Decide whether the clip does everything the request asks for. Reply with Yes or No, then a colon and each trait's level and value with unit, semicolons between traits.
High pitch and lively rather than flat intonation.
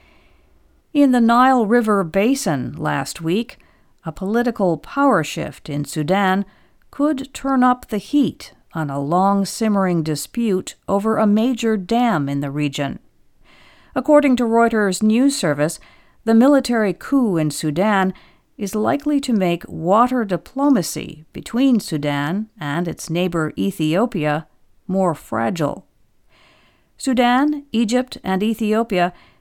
Yes: high, 200 Hz; wide, 6.9 semitones